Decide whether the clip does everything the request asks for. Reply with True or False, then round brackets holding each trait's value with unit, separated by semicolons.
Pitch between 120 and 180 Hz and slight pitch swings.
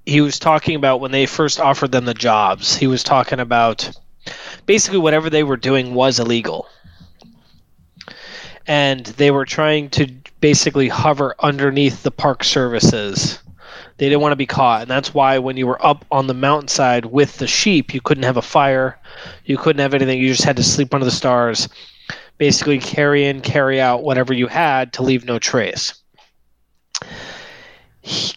True (135 Hz; 2.3 semitones)